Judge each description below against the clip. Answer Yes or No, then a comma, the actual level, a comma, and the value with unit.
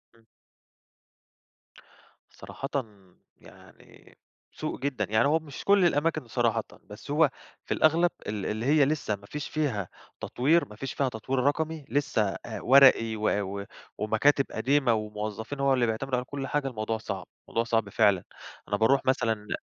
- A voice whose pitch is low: Yes, low, 125 Hz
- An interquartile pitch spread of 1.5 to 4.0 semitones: No, average, 4.8 semitones